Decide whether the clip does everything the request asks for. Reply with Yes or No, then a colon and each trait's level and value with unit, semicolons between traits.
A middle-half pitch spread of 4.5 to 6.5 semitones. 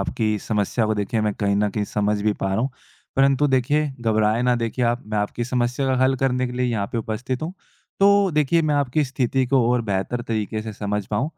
No: average, 3.7 semitones